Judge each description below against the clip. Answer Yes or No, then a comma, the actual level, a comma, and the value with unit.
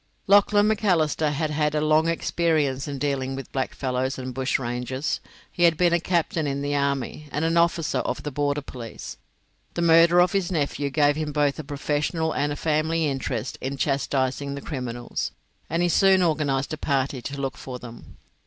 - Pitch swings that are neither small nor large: Yes, average, 3.3 semitones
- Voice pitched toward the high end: No, medium, 145 Hz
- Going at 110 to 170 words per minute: No, average, 180 wpm